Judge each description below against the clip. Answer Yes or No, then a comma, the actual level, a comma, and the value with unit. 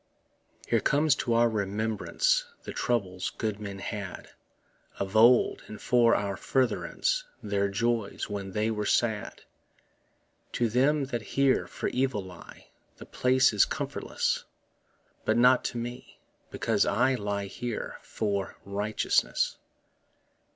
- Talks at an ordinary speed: No, slow, 130 wpm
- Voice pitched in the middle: No, low, 110 Hz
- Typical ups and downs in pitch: Yes, average, 3.5 semitones